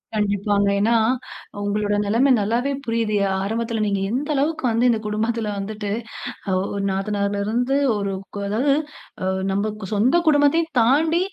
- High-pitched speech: Yes, high, 220 Hz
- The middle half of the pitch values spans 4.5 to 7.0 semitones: No, average, 3.9 semitones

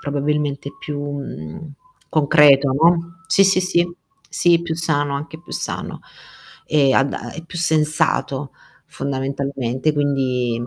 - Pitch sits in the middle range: Yes, medium, 145 Hz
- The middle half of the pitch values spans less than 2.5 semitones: No, average, 2.8 semitones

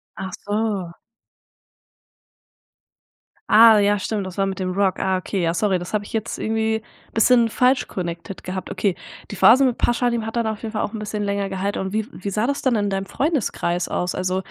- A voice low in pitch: No, high, 205 Hz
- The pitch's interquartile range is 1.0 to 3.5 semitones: Yes, average, 2.8 semitones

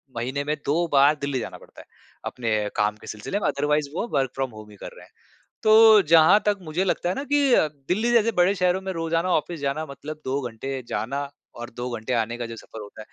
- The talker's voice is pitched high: No, medium, 145 Hz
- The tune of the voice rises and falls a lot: Yes, wide, 6.6 semitones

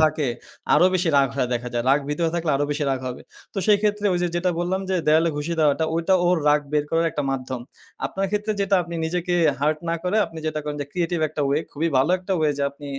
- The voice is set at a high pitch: No, medium, 160 Hz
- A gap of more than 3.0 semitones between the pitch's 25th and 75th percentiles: Yes, average, 3.4 semitones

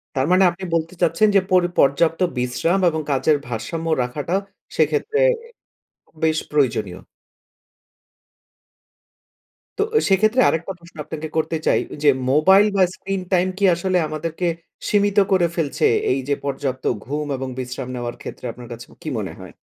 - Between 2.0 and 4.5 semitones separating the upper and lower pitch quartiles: No, average, 5.2 semitones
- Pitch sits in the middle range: Yes, medium, 160 Hz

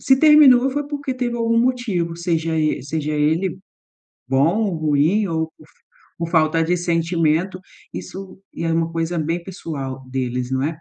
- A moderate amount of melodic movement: Yes, average, 4.0 semitones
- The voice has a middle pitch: Yes, medium, 165 Hz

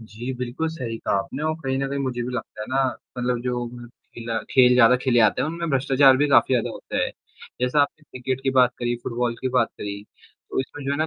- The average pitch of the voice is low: Yes, low, 125 Hz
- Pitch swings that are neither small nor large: No, narrow, 2.1 semitones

